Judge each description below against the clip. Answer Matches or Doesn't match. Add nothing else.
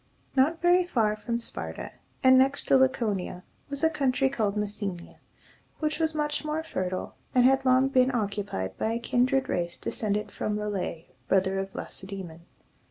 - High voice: Matches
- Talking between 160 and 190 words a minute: Matches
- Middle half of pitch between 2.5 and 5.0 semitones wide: Doesn't match